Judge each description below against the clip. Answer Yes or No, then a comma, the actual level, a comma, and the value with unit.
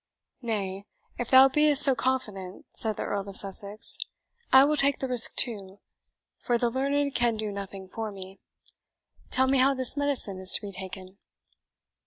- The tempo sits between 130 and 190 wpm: Yes, average, 170 wpm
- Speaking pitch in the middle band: No, high, 225 Hz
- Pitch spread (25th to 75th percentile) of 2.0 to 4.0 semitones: No, average, 5.1 semitones